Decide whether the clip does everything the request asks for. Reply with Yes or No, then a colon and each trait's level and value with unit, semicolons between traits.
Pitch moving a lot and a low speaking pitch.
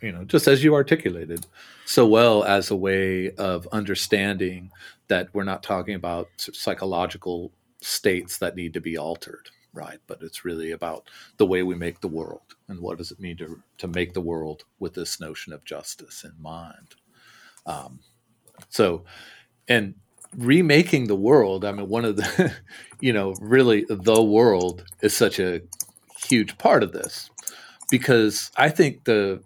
No: average, 3.8 semitones; very low, 95 Hz